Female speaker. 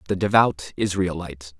No: male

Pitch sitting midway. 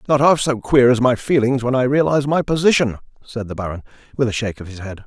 No: low, 125 Hz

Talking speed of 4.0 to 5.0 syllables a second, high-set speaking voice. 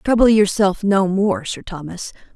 Yes: 4.4 syllables/s; high, 200 Hz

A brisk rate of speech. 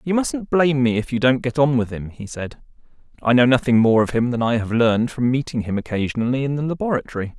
Yes: fast, 245 wpm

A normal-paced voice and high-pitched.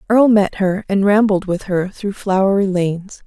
Yes: average, 185 wpm; high, 195 Hz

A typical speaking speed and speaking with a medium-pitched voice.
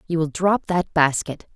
Yes: average, 195 wpm; medium, 165 Hz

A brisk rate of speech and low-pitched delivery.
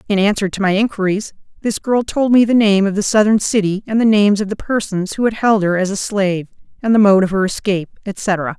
No: fast, 245 wpm; high, 205 Hz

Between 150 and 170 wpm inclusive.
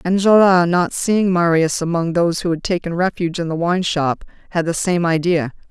No: average, 190 wpm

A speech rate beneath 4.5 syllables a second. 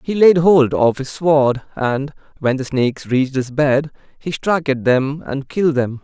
Yes: 4.3 syllables/s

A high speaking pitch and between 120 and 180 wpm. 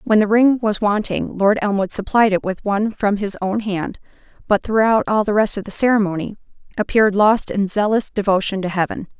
No: high, 205 Hz; average, 195 wpm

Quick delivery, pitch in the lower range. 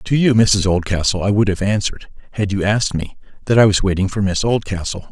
Yes: fast, 225 wpm; low, 100 Hz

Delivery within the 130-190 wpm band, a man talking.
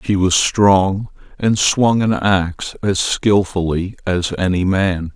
Yes: average, 140 wpm; male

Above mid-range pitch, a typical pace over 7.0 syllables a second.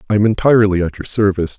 No: low, 100 Hz; 7.9 syllables/s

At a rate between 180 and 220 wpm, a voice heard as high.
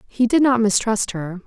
Yes: fast, 205 wpm; high, 220 Hz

